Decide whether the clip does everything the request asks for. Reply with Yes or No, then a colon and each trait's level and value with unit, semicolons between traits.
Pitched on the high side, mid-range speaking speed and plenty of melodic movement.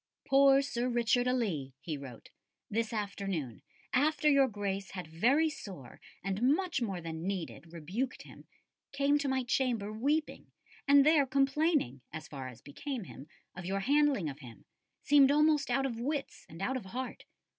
Yes: high, 235 Hz; average, 165 wpm; wide, 7.6 semitones